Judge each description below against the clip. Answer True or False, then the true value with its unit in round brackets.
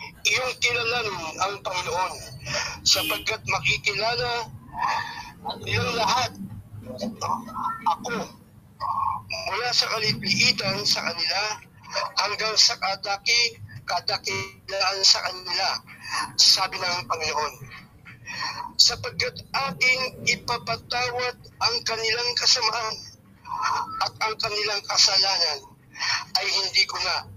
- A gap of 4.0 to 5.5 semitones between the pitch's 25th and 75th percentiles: True (4.4 semitones)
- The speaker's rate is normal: False (80 wpm)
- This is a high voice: True (220 Hz)